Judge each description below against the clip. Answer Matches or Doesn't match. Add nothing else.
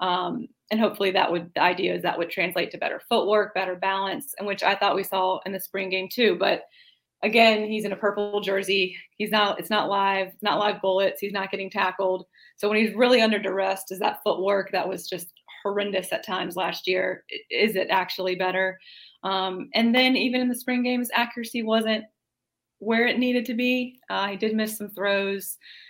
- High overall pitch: Matches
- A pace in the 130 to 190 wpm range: Doesn't match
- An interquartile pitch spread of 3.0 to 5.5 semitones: Doesn't match